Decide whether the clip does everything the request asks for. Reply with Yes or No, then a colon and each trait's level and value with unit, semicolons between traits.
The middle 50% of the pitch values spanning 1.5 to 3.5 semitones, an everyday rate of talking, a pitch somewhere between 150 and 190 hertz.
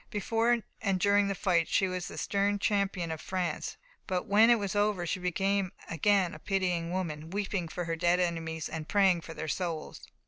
Yes: average, 3.0 semitones; average, 195 wpm; medium, 185 Hz